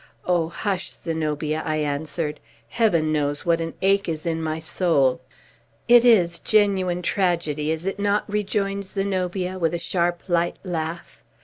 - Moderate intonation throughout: Yes, average, 3.5 semitones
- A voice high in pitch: No, medium, 170 Hz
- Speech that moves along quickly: No, average, 145 wpm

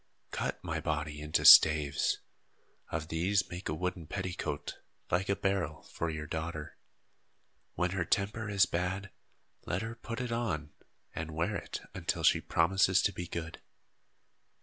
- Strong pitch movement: No, average, 3.8 semitones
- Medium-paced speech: Yes, average, 150 wpm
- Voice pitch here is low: Yes, very low, 90 Hz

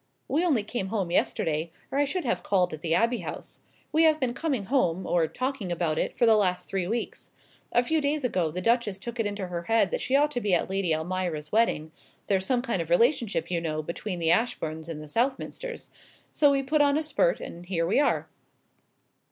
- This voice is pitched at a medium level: No, high, 205 Hz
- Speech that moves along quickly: Yes, fast, 220 wpm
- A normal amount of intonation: No, wide, 7.2 semitones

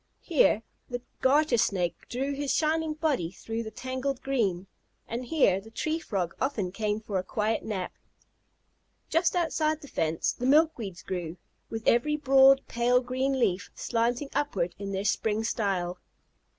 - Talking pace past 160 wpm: No, average, 150 wpm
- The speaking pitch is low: No, high, 235 Hz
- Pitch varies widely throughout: Yes, wide, 5.9 semitones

